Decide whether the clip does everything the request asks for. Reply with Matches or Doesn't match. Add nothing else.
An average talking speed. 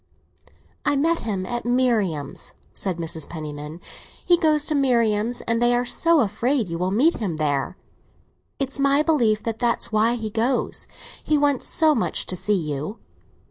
Matches